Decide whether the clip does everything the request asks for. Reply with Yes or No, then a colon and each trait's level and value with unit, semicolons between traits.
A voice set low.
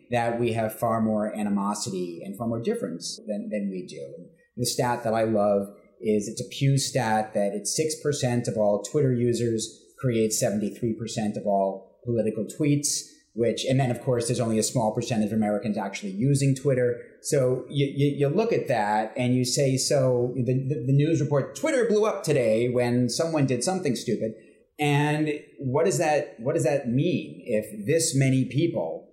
Yes: low, 120 Hz